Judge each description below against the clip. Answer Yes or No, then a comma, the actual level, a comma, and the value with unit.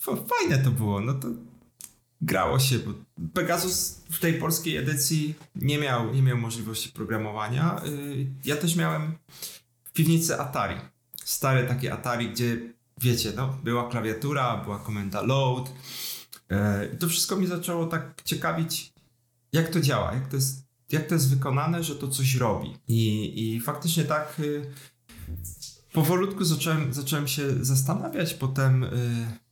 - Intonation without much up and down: No, average, 4.7 semitones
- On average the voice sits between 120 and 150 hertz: Yes, low, 135 Hz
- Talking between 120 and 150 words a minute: Yes, average, 135 wpm